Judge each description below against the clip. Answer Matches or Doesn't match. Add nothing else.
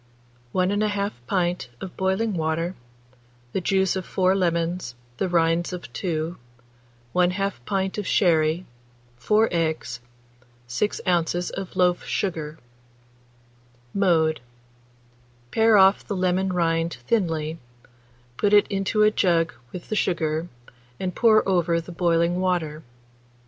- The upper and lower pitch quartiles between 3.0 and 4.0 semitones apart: Doesn't match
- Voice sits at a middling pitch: Matches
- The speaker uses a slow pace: Matches